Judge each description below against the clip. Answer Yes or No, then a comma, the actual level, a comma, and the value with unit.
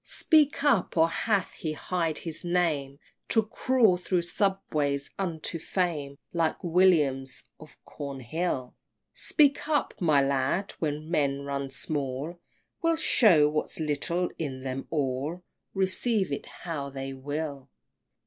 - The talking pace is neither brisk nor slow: No, slow, 130 wpm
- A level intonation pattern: No, average, 4.6 semitones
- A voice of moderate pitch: Yes, medium, 160 Hz